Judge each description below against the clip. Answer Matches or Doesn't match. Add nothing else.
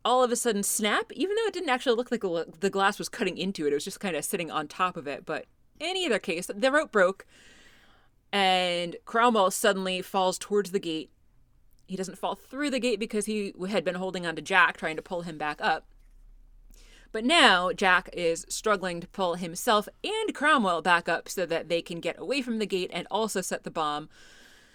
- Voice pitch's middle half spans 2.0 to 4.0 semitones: Doesn't match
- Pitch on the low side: Doesn't match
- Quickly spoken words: Matches